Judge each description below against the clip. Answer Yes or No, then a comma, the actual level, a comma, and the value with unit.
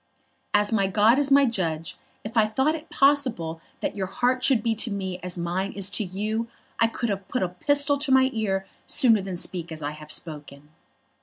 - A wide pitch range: Yes, wide, 5.7 semitones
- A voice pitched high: Yes, high, 205 Hz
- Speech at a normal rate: No, fast, 210 wpm